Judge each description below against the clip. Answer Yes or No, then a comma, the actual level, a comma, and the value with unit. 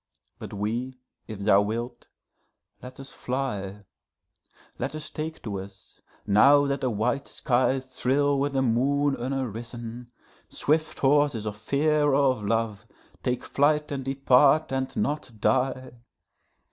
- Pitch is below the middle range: Yes, low, 130 Hz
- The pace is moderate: No, slow, 125 wpm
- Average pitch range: Yes, average, 3.6 semitones